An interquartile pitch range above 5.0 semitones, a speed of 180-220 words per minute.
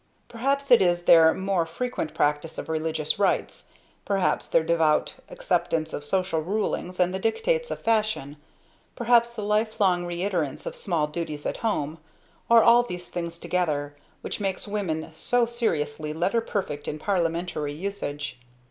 No: wide, 5.4 semitones; average, 150 wpm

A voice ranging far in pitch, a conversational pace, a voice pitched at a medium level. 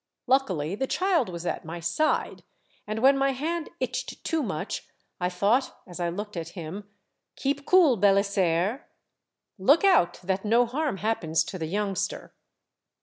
No: wide, 7.1 semitones; average, 155 wpm; high, 205 Hz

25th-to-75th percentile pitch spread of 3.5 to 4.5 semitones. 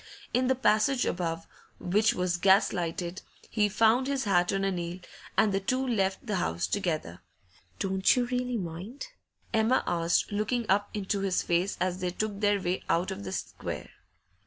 Yes: average, 3.8 semitones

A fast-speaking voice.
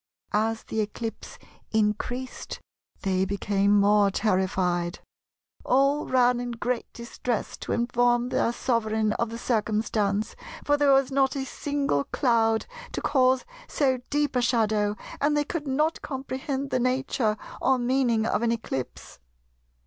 No: slow, 135 wpm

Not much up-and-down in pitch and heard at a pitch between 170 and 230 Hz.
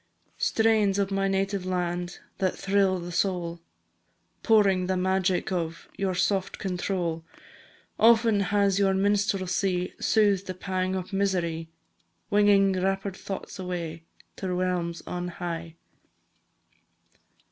Yes: narrow, 1.8 semitones; high, 190 Hz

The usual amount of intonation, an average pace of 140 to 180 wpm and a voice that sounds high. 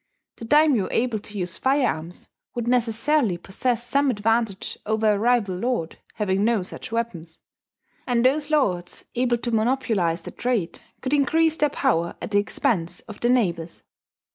Yes: average, 4.9 semitones; average, 155 wpm; high, 230 Hz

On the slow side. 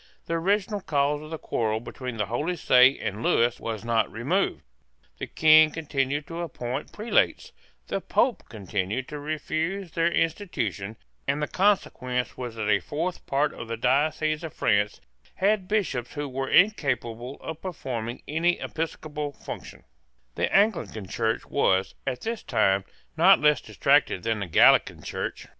No: average, 150 wpm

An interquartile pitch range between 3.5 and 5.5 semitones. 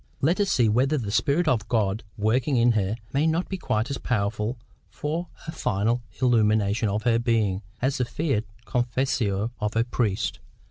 Yes: average, 4.1 semitones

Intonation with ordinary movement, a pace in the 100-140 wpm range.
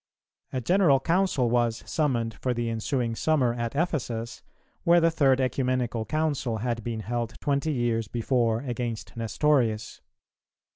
Yes: average, 3.6 semitones; slow, 135 wpm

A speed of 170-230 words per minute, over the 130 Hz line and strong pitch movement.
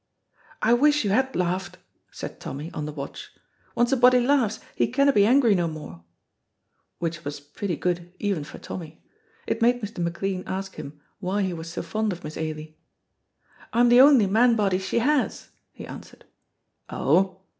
Yes: average, 175 wpm; high, 190 Hz; wide, 6.1 semitones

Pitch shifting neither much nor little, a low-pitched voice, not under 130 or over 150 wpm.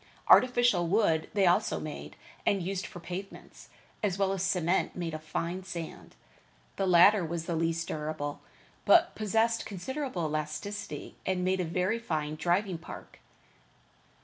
No: average, 3.4 semitones; medium, 180 Hz; average, 145 wpm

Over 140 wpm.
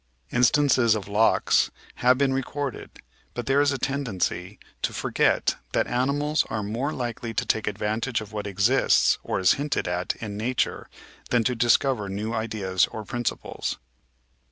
Yes: average, 155 wpm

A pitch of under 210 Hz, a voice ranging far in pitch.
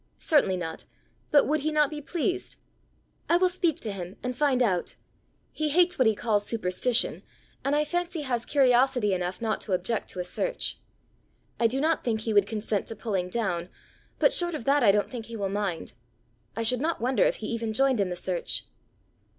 No: high, 235 Hz; wide, 6.4 semitones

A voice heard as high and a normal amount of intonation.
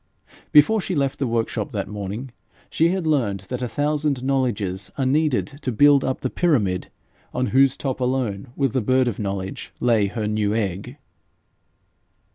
No: low, 125 Hz; average, 4.9 semitones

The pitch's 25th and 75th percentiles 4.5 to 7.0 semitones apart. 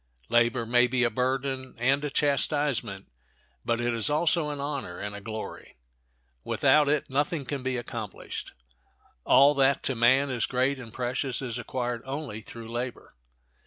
No: average, 2.9 semitones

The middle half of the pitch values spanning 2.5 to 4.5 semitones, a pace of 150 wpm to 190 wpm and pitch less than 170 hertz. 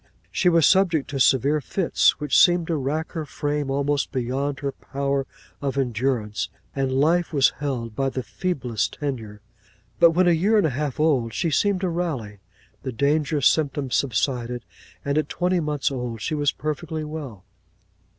Yes: average, 3.4 semitones; average, 170 wpm; medium, 140 Hz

